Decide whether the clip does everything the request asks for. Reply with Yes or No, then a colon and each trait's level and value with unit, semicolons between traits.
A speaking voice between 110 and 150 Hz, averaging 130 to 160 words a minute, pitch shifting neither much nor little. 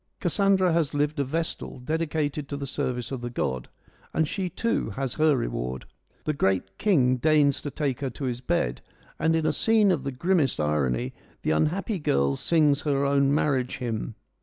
No: medium, 140 Hz; average, 185 wpm; average, 4.7 semitones